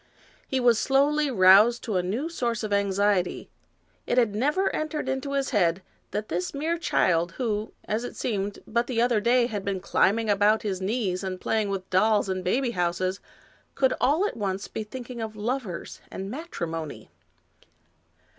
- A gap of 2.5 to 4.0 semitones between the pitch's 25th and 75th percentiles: No, average, 4.8 semitones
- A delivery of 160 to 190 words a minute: Yes, average, 170 wpm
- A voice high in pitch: Yes, high, 215 Hz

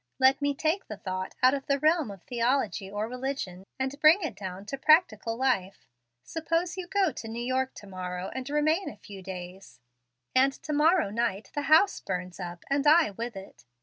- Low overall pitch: No, very high, 255 Hz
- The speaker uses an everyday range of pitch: No, wide, 7.4 semitones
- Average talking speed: Yes, average, 195 wpm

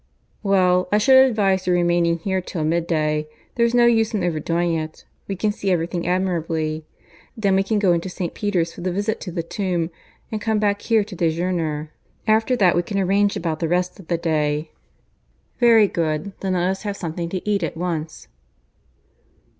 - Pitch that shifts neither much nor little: Yes, average, 3.5 semitones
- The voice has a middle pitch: Yes, medium, 180 Hz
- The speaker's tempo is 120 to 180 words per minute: No, average, 190 wpm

